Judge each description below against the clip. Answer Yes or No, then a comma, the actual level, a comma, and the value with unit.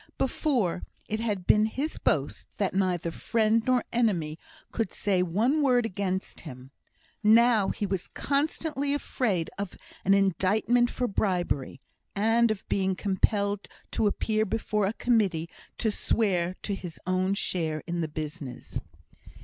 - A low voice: No, high, 200 Hz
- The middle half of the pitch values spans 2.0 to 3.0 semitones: No, average, 3.9 semitones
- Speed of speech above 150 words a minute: No, average, 140 wpm